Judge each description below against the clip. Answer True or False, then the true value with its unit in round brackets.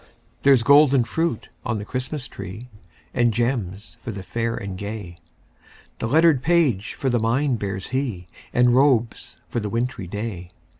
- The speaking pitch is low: True (115 Hz)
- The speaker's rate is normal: True (155 wpm)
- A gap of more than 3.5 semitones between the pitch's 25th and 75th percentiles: True (4.5 semitones)